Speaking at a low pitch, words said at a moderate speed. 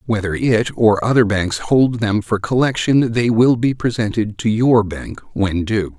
Yes: low, 110 Hz; average, 180 wpm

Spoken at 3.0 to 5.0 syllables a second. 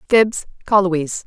Yes: 4.5 syllables/s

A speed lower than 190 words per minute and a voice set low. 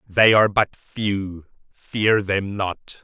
Yes: average, 140 wpm; low, 100 Hz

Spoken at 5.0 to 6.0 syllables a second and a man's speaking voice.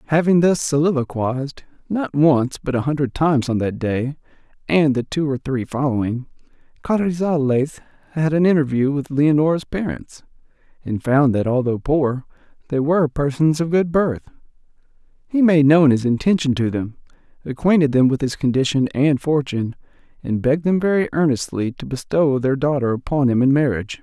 Yes: 5.2 syllables/s; male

